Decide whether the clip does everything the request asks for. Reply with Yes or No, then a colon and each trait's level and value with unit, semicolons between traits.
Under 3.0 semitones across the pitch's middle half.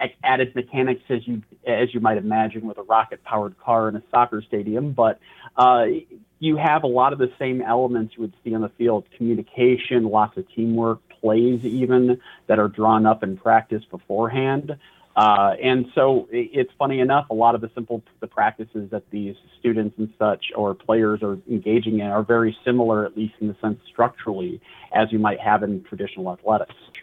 Yes: narrow, 2.5 semitones